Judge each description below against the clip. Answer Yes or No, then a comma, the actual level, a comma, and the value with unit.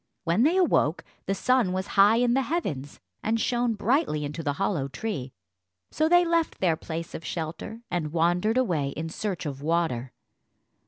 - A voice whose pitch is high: No, medium, 180 Hz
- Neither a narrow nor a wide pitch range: No, wide, 7.2 semitones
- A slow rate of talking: No, average, 170 wpm